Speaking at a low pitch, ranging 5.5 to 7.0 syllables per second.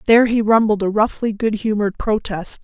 No: high, 215 Hz; 5.8 syllables/s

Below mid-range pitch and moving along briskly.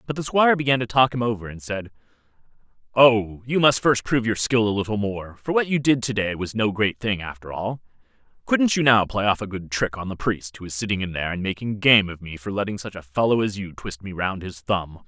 Yes: low, 105 Hz; fast, 260 wpm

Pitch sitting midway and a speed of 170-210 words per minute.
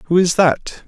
Yes: medium, 165 Hz; fast, 205 wpm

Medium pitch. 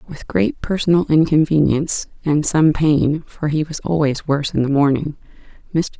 Yes: medium, 155 Hz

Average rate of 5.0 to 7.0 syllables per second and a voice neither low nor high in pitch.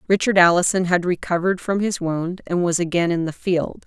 Yes: 5.5 syllables/s; medium, 175 Hz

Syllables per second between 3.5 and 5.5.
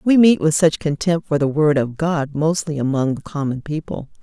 Yes: 5.0 syllables/s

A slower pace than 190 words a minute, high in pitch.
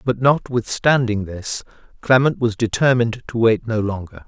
No: average, 140 wpm; low, 115 Hz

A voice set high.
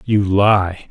No: low, 100 Hz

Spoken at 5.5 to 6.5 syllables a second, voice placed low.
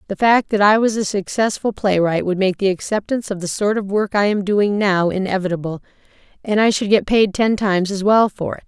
No: 5.6 syllables/s; high, 200 Hz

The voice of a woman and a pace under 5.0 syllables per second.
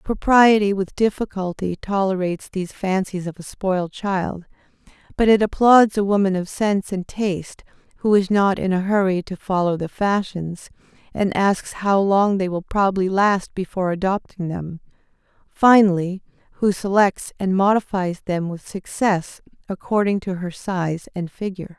Yes: female; 4.7 syllables/s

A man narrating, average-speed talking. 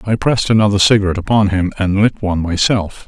Yes: male; average, 195 wpm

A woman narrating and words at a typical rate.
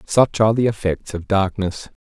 No: male; average, 175 wpm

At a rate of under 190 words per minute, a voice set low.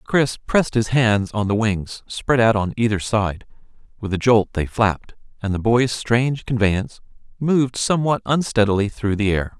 Yes: average, 175 wpm; low, 115 Hz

